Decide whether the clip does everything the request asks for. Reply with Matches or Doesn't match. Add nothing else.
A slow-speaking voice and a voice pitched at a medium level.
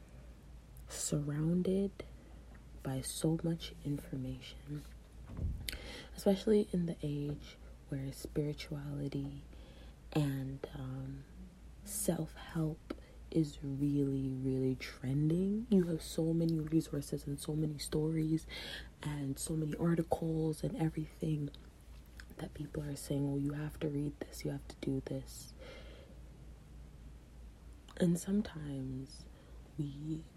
Matches